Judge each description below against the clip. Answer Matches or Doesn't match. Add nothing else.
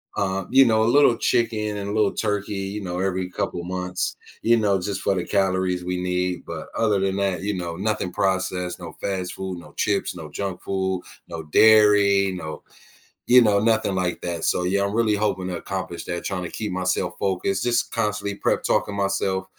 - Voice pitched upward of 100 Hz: Doesn't match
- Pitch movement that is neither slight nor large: Doesn't match